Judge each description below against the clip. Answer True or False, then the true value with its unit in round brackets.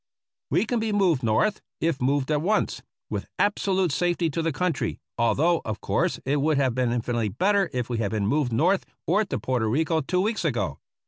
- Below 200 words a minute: False (205 wpm)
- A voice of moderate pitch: True (150 Hz)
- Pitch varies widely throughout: True (6.8 semitones)